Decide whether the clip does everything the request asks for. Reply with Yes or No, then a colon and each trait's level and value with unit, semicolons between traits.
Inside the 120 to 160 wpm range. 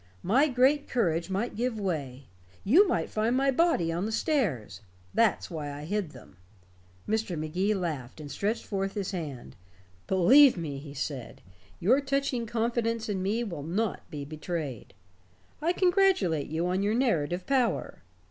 Yes: average, 155 wpm